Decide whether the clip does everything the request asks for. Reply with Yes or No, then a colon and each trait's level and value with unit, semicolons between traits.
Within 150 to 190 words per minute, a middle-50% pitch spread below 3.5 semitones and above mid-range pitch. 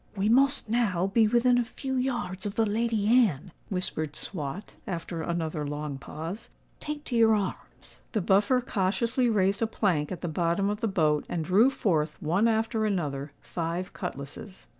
No: average, 170 wpm; average, 5.3 semitones; high, 195 Hz